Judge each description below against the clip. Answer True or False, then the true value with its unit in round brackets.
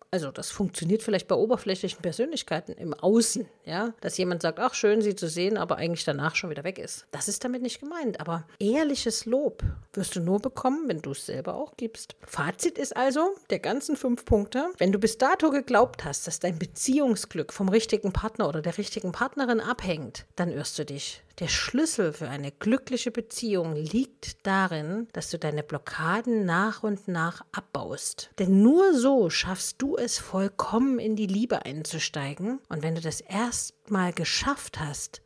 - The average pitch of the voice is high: True (210 Hz)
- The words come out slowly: False (180 wpm)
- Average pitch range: False (6.3 semitones)